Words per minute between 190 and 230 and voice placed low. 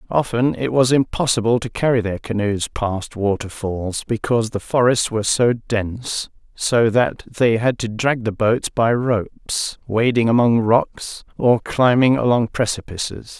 No: average, 150 wpm; low, 115 Hz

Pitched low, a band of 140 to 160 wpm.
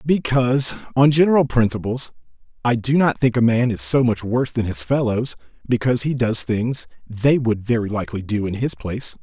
No: low, 120 Hz; average, 190 wpm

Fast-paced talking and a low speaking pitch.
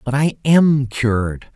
No: average, 155 wpm; low, 130 Hz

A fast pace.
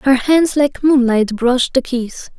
No: average, 175 wpm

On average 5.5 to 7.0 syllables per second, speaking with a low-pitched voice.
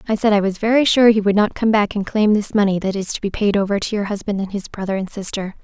No: 6.5 syllables/s; high, 205 Hz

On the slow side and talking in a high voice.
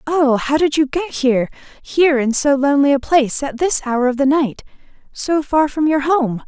No: fast, 205 wpm; very high, 280 Hz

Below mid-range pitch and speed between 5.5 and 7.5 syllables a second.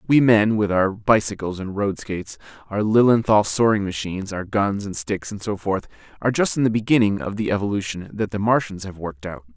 Yes: low, 100 Hz; 5.7 syllables/s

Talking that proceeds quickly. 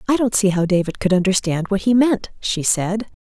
Yes: fast, 225 wpm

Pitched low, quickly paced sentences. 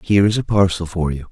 Yes: very low, 90 Hz; fast, 275 wpm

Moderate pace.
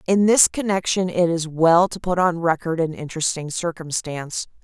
Yes: average, 170 wpm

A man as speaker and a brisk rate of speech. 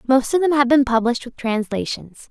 No: female; fast, 210 wpm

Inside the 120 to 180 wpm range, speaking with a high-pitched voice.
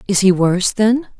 No: average, 200 wpm; high, 200 Hz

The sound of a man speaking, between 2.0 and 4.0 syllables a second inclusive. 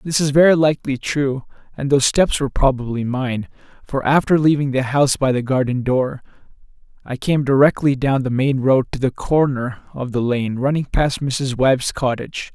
No: male; 5.1 syllables/s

